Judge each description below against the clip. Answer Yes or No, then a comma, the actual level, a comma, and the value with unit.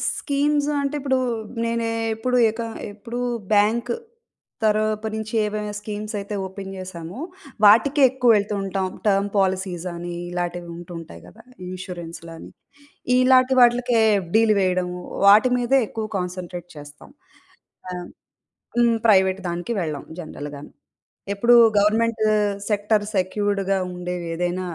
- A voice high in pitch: Yes, high, 205 Hz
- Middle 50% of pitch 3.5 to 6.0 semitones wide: Yes, average, 4.2 semitones